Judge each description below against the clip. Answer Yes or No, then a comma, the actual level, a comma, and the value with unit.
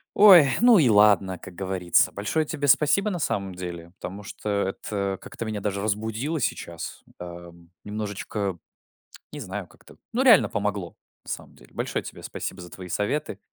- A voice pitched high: No, low, 105 Hz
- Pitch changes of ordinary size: No, wide, 6.2 semitones